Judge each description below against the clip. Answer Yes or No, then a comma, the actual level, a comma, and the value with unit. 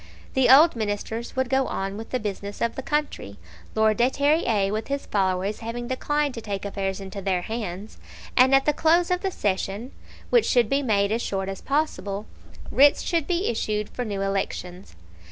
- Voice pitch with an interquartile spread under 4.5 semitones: No, wide, 5.4 semitones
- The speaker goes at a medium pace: Yes, average, 190 wpm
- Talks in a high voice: Yes, high, 225 Hz